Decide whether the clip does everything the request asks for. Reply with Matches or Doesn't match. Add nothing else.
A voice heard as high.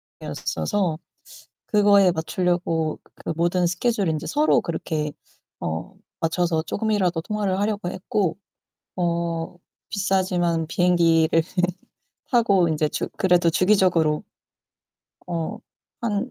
Doesn't match